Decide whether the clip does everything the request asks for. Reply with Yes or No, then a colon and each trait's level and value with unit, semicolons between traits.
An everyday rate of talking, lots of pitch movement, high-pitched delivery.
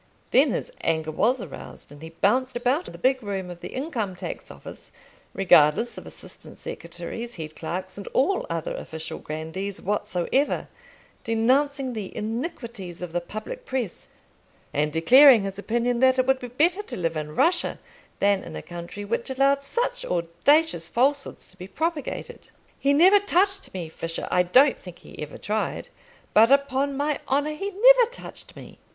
Yes: average, 165 wpm; wide, 8.0 semitones; high, 235 Hz